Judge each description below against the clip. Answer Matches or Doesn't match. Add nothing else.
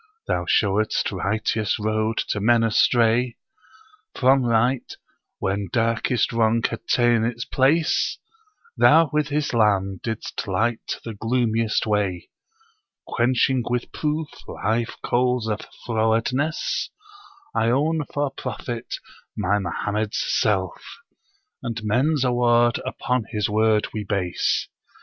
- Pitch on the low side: Matches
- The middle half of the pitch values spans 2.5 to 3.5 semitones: Matches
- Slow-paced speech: Matches